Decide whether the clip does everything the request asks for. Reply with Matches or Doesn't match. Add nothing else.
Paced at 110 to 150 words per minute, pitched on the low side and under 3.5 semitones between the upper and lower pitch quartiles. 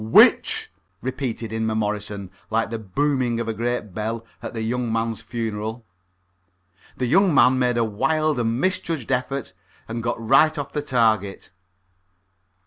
Matches